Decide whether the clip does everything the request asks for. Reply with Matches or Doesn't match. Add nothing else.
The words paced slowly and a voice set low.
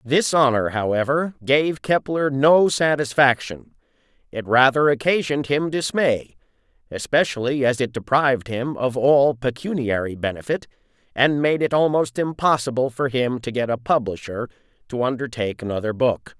Matches